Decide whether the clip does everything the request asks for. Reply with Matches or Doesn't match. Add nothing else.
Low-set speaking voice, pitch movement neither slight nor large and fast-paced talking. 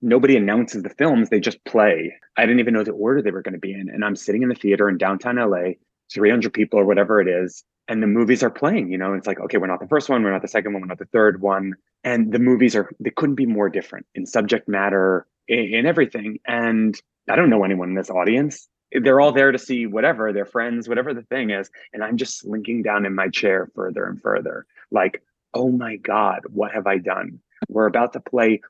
Matches